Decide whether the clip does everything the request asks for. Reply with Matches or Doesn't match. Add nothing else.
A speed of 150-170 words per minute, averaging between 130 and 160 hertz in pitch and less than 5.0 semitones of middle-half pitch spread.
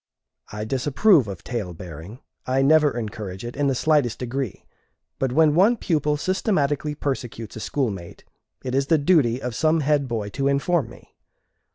Matches